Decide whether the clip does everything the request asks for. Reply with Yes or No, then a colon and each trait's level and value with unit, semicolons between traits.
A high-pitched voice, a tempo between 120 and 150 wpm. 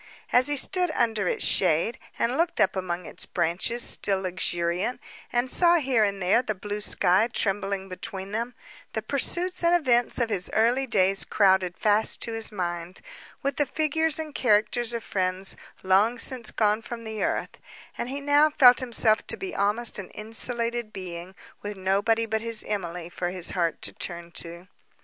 No: high, 215 Hz; average, 175 wpm